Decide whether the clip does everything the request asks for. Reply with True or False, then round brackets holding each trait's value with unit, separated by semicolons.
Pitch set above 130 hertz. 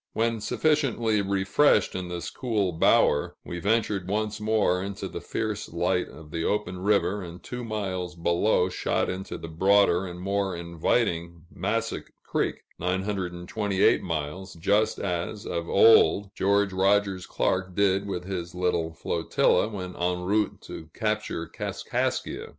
False (95 Hz)